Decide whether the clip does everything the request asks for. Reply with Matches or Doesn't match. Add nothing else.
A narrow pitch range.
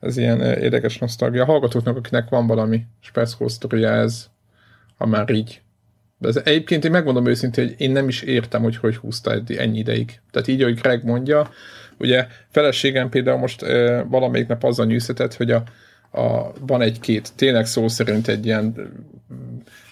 Matches